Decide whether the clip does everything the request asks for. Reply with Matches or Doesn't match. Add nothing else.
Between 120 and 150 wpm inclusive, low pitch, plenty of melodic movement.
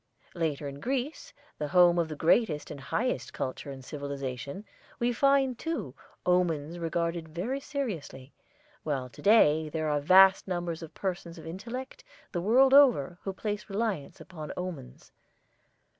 Doesn't match